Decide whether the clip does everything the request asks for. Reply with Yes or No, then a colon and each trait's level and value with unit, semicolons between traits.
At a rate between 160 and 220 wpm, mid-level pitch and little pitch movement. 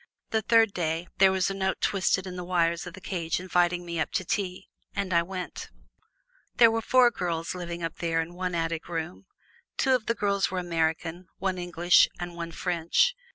Yes: average, 200 wpm; medium, 180 Hz; narrow, 2.2 semitones